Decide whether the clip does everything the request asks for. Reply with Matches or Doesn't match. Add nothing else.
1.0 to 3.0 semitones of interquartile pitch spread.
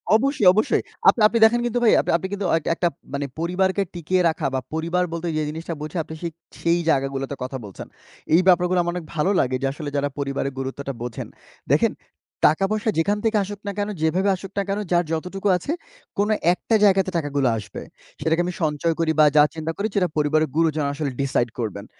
Doesn't match